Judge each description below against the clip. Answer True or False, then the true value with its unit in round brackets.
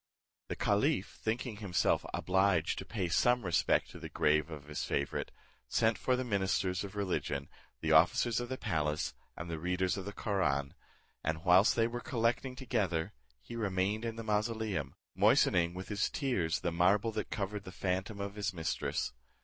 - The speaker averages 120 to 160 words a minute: False (175 wpm)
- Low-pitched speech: True (95 Hz)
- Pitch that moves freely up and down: False (4.4 semitones)